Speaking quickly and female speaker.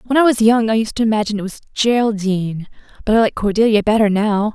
Yes: fast, 225 wpm; female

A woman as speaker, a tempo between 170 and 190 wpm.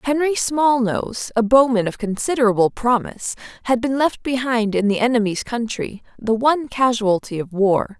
No: female; average, 150 wpm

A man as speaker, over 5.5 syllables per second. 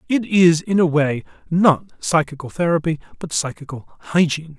No: male; 5.2 syllables/s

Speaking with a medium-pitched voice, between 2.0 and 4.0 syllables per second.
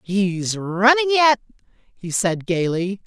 No: high, 210 Hz; 3.1 syllables/s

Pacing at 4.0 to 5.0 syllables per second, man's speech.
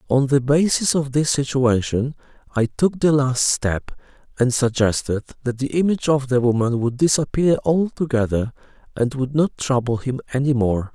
Yes: 4.8 syllables/s; male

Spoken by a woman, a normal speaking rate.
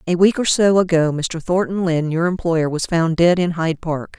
No: female; fast, 230 wpm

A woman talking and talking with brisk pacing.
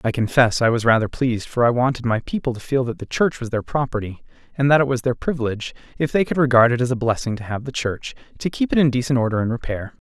No: male; fast, 270 wpm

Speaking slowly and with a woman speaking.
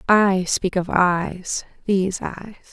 Yes: slow, 110 wpm; female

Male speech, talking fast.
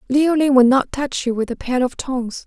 No: female; fast, 245 wpm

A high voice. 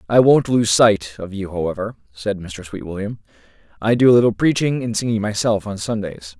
No: low, 105 Hz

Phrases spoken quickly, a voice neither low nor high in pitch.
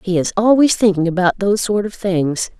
No: fast, 210 wpm; high, 195 Hz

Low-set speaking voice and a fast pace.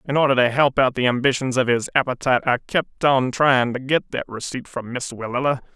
Yes: low, 130 Hz; fast, 220 wpm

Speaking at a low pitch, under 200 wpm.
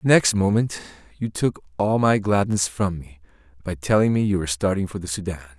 No: very low, 95 Hz; fast, 205 wpm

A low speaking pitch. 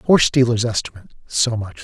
Yes: low, 115 Hz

